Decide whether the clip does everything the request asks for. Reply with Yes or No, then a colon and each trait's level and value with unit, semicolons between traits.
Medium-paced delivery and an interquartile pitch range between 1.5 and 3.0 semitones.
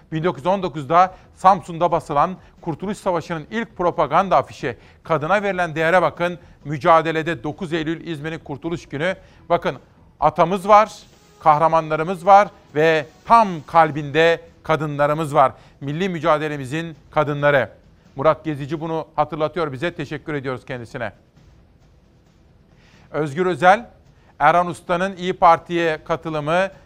Yes: average, 105 wpm; narrow, 2.5 semitones